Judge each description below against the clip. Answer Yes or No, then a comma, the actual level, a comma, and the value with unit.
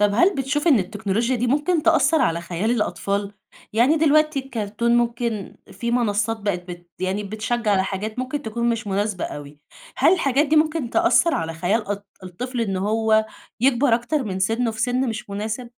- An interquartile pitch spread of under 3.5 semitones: No, average, 4.2 semitones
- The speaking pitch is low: No, high, 225 Hz